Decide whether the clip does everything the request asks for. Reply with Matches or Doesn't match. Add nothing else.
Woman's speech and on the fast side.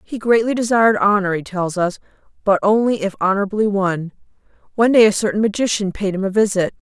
Doesn't match